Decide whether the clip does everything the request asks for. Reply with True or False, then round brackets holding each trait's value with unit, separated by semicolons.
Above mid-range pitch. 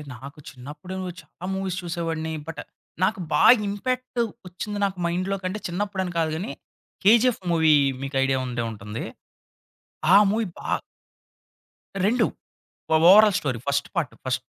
False (175 Hz)